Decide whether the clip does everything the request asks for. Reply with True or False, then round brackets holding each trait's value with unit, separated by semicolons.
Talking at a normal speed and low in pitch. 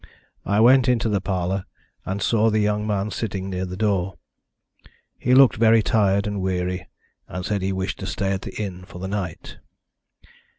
True (180 wpm; 100 Hz)